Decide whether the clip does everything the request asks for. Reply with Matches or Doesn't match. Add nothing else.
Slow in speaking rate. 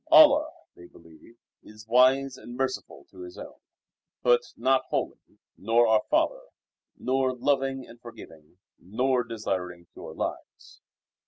Matches